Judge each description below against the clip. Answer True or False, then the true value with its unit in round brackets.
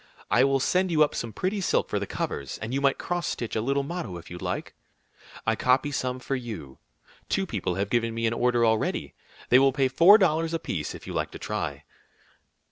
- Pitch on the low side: True (130 Hz)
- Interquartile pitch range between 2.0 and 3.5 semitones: False (5.3 semitones)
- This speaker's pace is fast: True (215 wpm)